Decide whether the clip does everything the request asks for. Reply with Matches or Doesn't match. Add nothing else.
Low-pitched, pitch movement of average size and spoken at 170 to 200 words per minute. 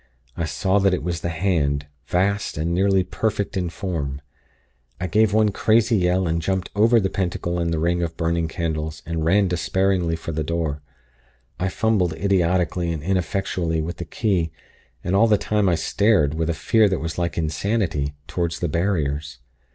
Matches